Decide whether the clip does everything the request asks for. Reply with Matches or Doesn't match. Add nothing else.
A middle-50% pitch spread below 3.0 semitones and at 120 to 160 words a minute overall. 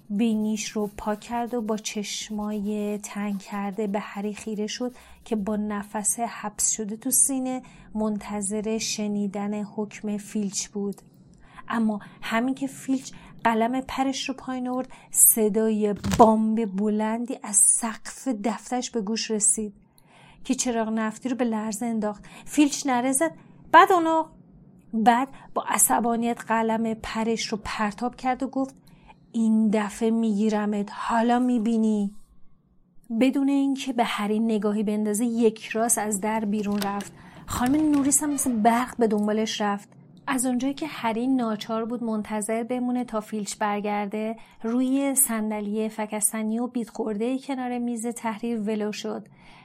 Matches